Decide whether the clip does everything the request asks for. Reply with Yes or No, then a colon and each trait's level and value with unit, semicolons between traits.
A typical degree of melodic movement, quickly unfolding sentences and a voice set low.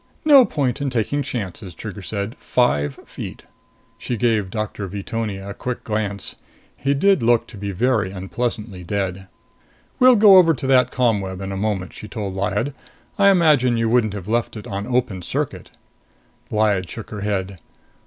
No: average, 4.3 semitones; average, 160 wpm; low, 110 Hz